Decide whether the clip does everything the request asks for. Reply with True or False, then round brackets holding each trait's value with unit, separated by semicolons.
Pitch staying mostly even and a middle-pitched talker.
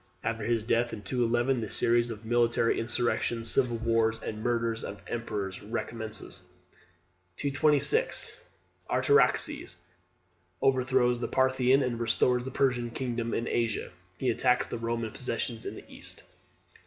False (1.6 semitones; 120 Hz)